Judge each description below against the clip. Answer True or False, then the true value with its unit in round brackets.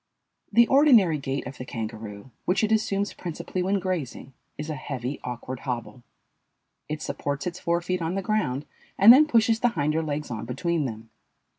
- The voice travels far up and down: True (7.0 semitones)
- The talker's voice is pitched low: False (155 Hz)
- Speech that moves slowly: False (175 wpm)